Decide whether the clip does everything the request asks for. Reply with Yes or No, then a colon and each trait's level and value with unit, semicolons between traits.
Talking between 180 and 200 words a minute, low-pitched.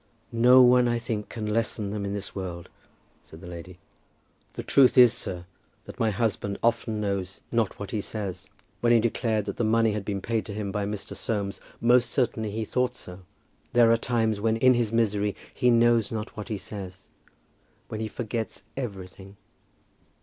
Yes: average, 185 wpm; low, 110 Hz